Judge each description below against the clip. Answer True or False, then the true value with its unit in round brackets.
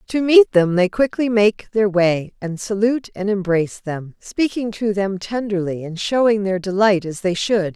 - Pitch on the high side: True (200 Hz)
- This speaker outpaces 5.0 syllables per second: False (4.6 syllables/s)